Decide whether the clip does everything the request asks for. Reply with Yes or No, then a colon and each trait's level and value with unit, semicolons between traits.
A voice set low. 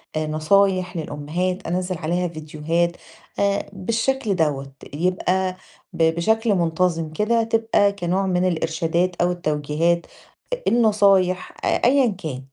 No: medium, 180 Hz